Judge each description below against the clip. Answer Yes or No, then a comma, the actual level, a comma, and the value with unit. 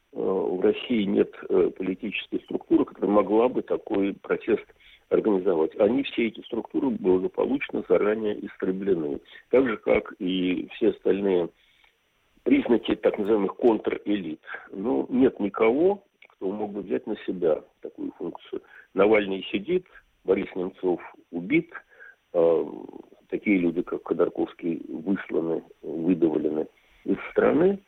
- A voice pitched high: Yes, very high, 370 Hz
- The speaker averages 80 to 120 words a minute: Yes, slow, 110 wpm